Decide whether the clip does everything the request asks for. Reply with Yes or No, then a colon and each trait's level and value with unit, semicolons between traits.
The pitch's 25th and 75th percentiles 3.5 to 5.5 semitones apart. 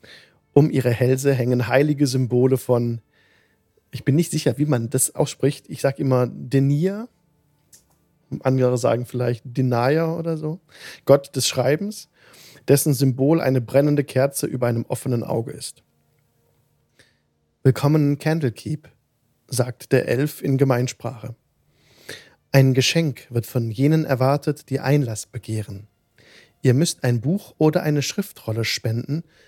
No: average, 3.0 semitones